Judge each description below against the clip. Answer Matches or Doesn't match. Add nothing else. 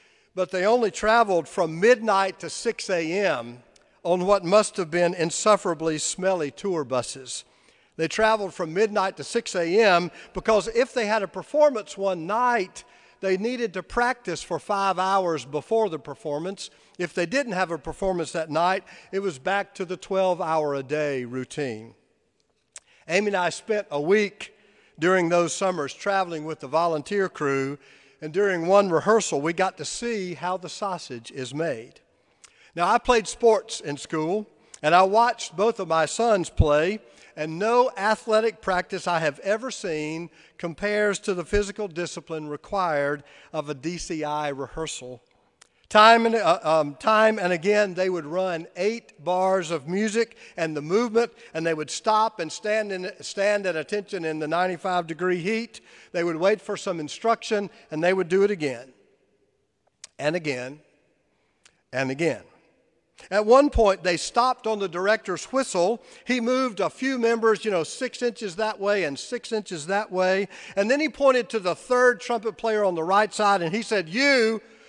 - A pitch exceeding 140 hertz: Matches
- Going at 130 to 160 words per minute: Doesn't match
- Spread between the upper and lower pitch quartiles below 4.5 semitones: Doesn't match